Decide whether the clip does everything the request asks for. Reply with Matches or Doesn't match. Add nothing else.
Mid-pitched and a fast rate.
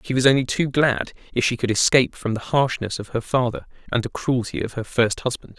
Doesn't match